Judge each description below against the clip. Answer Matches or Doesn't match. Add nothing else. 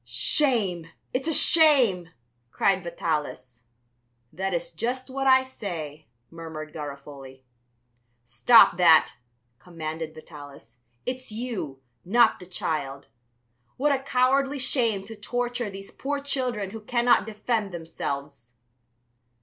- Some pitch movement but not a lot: Doesn't match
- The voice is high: Matches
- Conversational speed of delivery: Doesn't match